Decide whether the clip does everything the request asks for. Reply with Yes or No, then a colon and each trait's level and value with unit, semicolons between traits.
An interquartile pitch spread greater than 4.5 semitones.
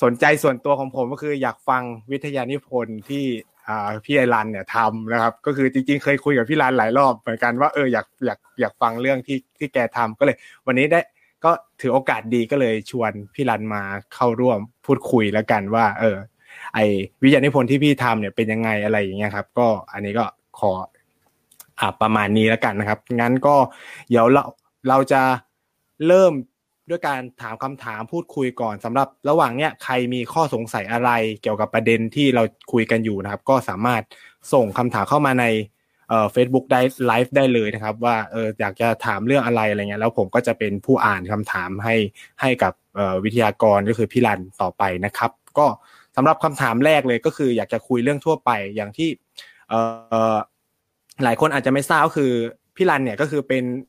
No: average, 3.8 semitones